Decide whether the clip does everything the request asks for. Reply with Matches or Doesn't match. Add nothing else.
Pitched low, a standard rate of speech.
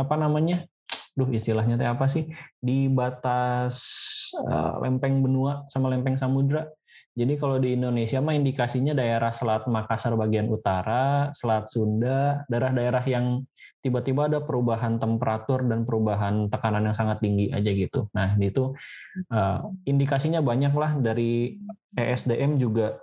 Matches